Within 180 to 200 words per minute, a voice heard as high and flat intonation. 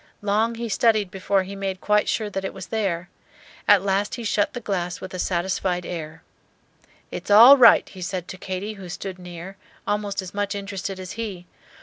Yes: average, 195 wpm; high, 195 Hz; narrow, 2.1 semitones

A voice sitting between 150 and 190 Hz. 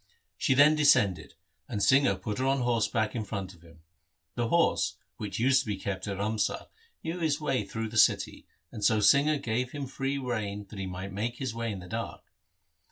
No: low, 110 Hz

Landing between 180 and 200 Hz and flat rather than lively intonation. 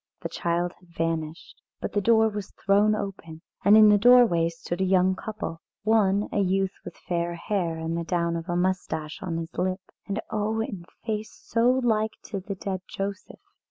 No: high, 190 Hz; average, 3.7 semitones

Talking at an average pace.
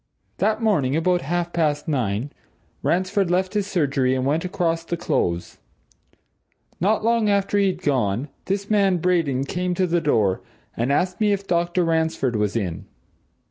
Yes: average, 155 wpm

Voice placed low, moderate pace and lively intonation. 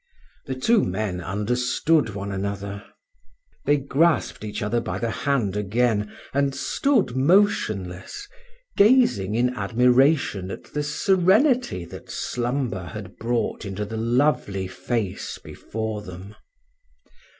No: low, 115 Hz; slow, 115 wpm; wide, 5.9 semitones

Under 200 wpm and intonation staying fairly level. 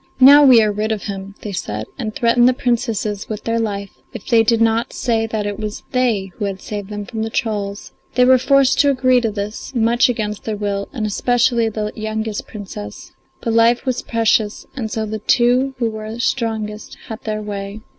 No: fast, 205 wpm; narrow, 2.3 semitones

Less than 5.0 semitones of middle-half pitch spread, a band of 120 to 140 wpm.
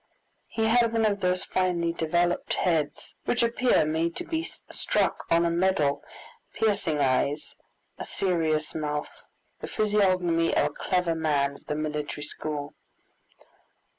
Yes: average, 4.1 semitones; slow, 135 wpm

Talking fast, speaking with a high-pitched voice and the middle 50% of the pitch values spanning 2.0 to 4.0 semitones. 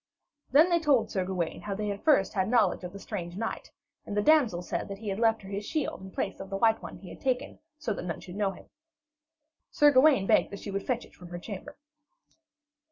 No: fast, 240 wpm; high, 205 Hz; average, 4.6 semitones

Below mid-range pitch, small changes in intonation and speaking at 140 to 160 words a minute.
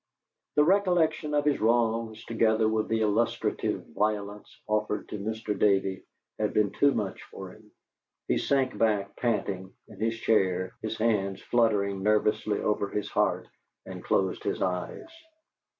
Yes: low, 110 Hz; narrow, 2.3 semitones; average, 145 wpm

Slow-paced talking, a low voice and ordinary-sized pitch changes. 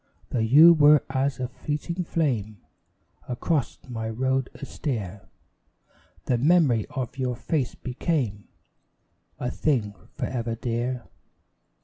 Yes: slow, 110 wpm; low, 125 Hz; average, 4.0 semitones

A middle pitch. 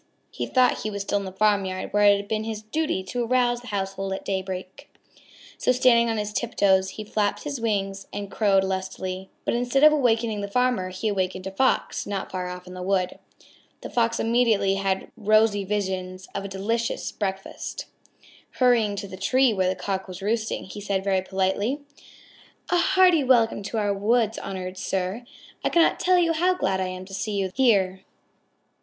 No: high, 205 Hz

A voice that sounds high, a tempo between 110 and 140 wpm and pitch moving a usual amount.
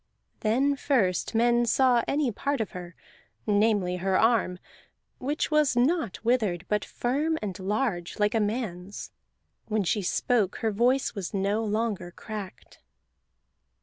Yes: high, 220 Hz; slow, 135 wpm; average, 4.0 semitones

